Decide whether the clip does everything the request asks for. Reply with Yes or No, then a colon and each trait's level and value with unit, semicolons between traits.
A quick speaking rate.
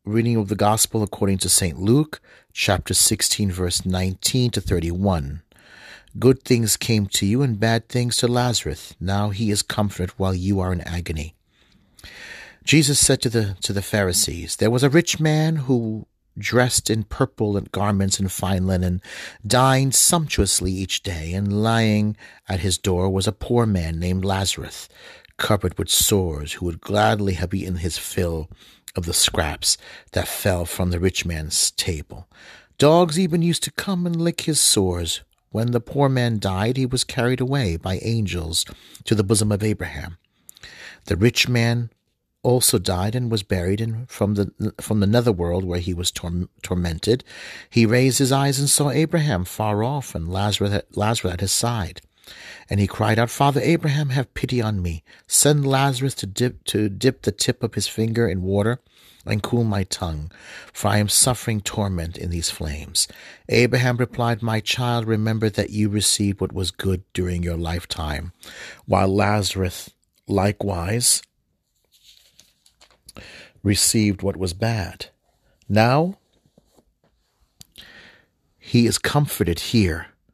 No: average, 155 wpm